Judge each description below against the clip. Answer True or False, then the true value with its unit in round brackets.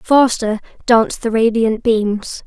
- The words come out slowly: True (120 wpm)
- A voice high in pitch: True (225 Hz)